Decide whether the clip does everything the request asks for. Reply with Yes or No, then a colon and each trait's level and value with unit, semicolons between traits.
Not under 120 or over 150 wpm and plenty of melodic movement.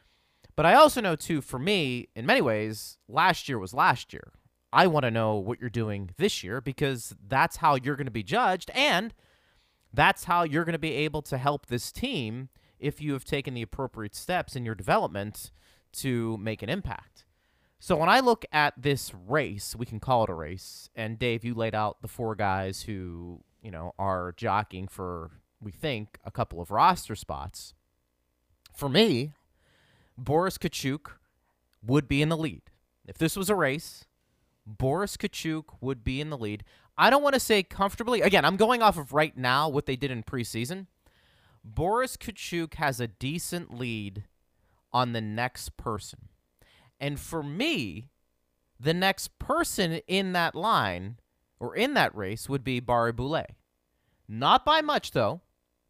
No: average, 175 wpm; wide, 7.6 semitones